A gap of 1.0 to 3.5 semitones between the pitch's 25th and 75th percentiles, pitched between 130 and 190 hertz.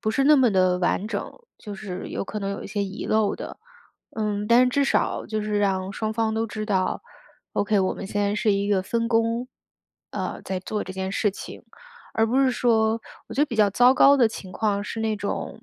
No: narrow, 2.4 semitones; high, 215 Hz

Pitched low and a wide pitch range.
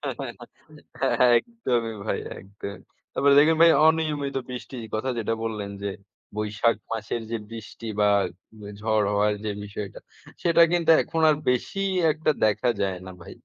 Yes: low, 115 Hz; wide, 6.4 semitones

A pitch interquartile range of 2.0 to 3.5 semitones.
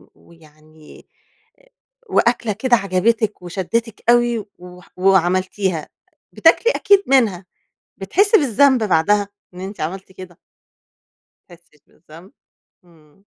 No: average, 4.8 semitones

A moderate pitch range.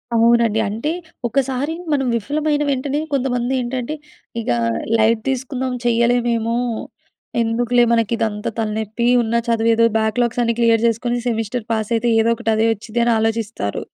No: narrow, 1.7 semitones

